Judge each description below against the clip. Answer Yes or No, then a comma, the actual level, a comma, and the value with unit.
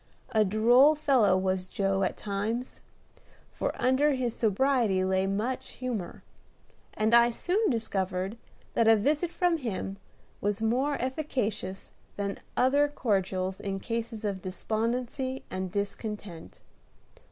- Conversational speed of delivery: No, slow, 120 wpm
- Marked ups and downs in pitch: No, average, 4.9 semitones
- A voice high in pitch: Yes, high, 220 Hz